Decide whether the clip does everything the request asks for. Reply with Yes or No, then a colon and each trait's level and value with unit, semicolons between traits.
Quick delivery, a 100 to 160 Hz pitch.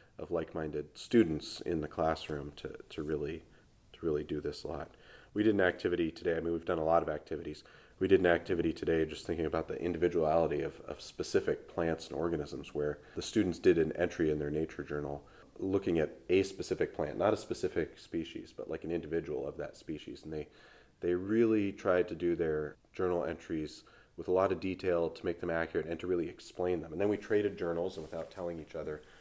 No: fast, 210 wpm; very low, 85 Hz